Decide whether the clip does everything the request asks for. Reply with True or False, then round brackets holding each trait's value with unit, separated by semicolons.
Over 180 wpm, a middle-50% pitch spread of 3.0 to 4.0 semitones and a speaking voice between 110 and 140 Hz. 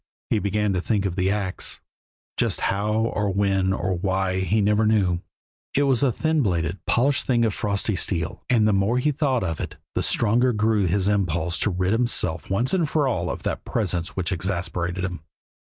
False (190 wpm; 3.4 semitones; 100 Hz)